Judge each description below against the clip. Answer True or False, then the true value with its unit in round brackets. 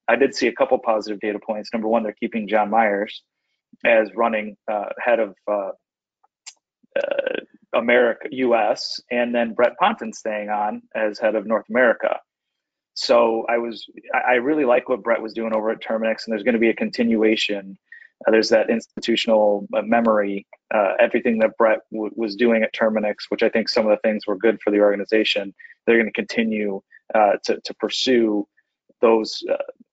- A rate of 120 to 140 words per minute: False (175 wpm)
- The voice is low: True (110 Hz)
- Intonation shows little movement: True (1.6 semitones)